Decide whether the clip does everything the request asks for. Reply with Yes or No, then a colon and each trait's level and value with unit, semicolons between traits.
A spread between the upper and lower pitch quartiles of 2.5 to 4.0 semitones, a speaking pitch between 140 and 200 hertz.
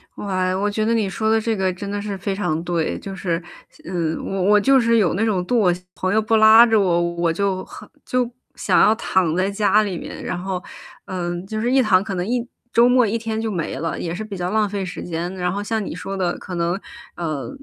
Yes: average, 3.4 semitones; high, 195 Hz